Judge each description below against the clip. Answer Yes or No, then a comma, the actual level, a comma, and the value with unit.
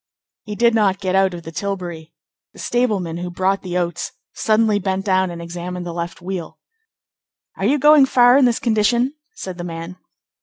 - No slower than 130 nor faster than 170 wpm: No, average, 185 wpm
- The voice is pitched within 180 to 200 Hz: Yes, high, 190 Hz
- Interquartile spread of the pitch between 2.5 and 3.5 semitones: No, average, 4.0 semitones